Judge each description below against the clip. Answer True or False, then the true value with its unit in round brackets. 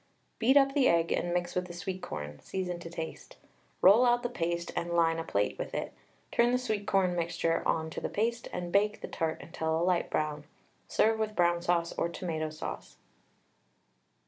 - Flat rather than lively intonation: False (4.1 semitones)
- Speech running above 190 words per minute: True (200 wpm)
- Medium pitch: True (175 Hz)